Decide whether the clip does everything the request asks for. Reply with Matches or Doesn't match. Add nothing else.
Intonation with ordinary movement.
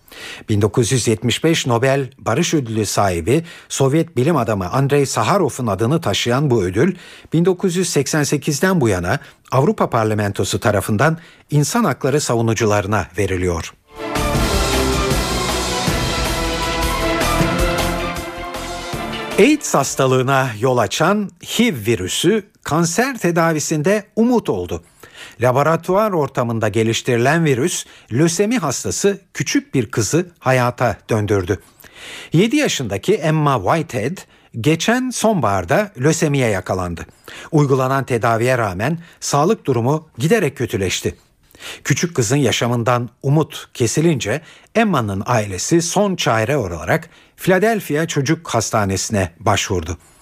Doesn't match